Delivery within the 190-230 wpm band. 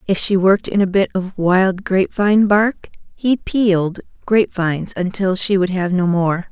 Yes: average, 195 wpm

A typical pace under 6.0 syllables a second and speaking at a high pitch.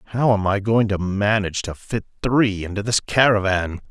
No: 5.0 syllables/s; low, 105 Hz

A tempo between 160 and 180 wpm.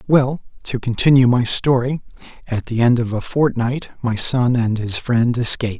Yes: average, 165 wpm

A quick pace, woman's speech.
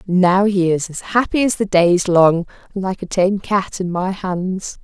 Yes: fast, 225 wpm; female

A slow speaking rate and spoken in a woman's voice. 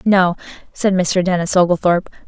Yes: slow, 130 wpm; female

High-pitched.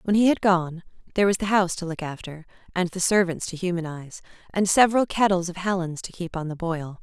No: medium, 180 Hz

